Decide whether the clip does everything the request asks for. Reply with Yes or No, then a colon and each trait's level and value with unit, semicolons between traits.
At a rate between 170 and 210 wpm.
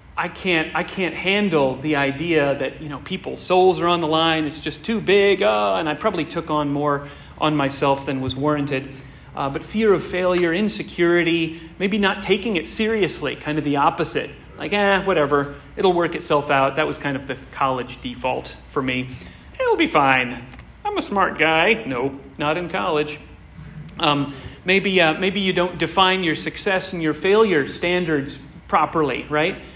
Yes: average, 180 wpm